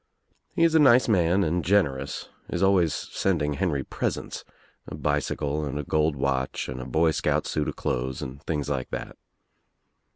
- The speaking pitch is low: Yes, very low, 75 Hz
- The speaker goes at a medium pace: Yes, average, 170 wpm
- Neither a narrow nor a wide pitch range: Yes, average, 4.4 semitones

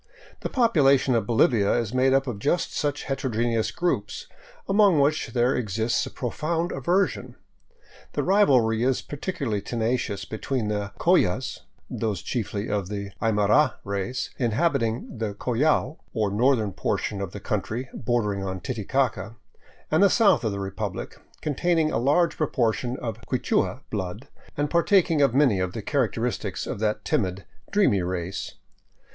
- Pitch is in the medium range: No, low, 120 Hz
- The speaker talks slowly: No, average, 145 wpm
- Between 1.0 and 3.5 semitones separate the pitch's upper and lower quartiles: No, wide, 5.5 semitones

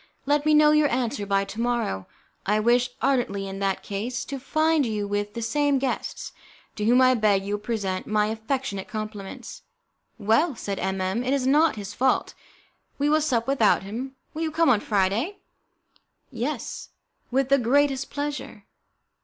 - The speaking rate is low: No, average, 170 wpm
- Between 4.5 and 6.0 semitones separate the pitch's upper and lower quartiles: Yes, average, 5.1 semitones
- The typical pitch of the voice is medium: No, high, 240 Hz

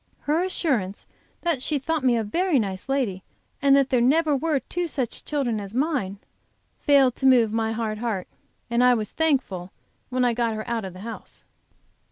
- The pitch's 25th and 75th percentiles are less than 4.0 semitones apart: No, average, 4.6 semitones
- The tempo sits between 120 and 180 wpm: No, average, 190 wpm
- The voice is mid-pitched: No, very high, 250 Hz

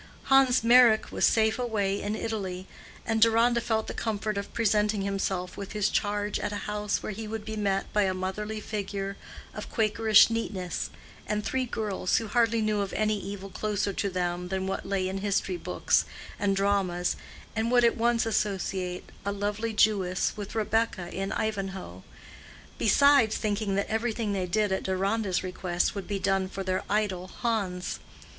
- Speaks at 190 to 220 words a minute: No, average, 170 wpm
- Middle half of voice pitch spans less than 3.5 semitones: Yes, narrow, 2.4 semitones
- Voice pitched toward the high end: Yes, high, 205 Hz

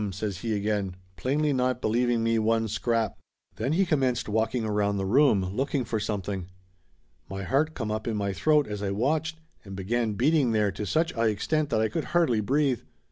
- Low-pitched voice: Yes, low, 115 Hz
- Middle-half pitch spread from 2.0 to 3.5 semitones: No, average, 4.8 semitones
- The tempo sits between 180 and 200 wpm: Yes, average, 195 wpm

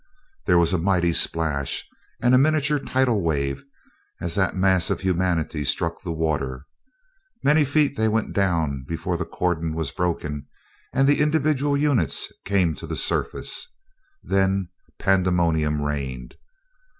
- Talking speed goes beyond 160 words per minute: No, average, 140 wpm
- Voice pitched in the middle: No, very low, 90 Hz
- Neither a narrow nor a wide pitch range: No, wide, 5.8 semitones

